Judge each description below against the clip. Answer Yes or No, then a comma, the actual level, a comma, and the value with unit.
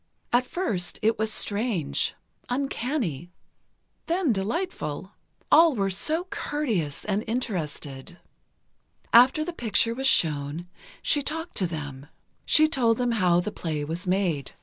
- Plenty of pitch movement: Yes, wide, 7.9 semitones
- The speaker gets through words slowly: Yes, slow, 125 wpm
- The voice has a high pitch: Yes, high, 210 Hz